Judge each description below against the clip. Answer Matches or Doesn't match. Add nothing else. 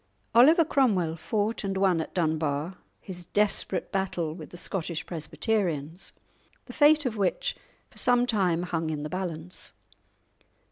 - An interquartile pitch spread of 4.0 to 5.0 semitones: Matches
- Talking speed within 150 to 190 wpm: Doesn't match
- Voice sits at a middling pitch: Matches